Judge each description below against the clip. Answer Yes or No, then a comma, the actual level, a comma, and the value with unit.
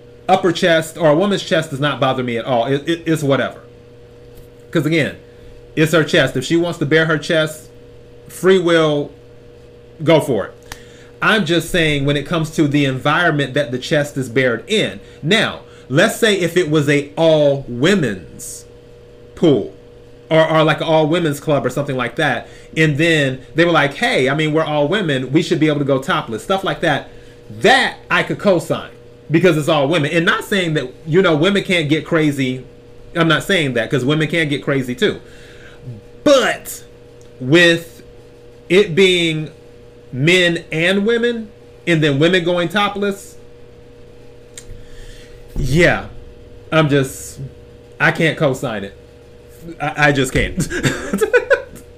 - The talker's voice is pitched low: No, medium, 145 Hz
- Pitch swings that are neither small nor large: No, wide, 5.7 semitones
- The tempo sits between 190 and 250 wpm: No, average, 160 wpm